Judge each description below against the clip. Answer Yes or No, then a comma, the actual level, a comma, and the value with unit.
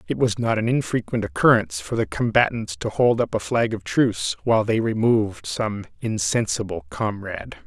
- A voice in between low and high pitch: No, low, 115 Hz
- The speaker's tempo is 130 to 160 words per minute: No, average, 170 wpm